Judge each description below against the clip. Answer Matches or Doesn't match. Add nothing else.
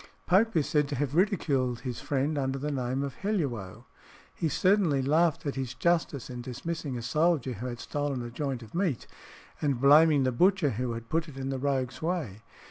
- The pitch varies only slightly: Doesn't match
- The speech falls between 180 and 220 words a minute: Matches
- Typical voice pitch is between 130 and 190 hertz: Matches